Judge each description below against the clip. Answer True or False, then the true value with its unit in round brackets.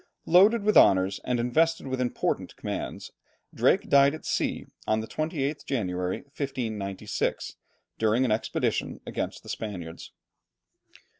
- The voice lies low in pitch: True (125 Hz)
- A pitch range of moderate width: False (5.7 semitones)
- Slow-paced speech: True (125 wpm)